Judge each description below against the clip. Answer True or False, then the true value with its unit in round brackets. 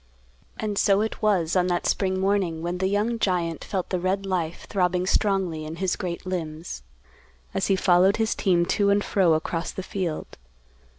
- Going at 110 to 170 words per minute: False (180 wpm)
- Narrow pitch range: True (2.3 semitones)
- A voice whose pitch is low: False (185 Hz)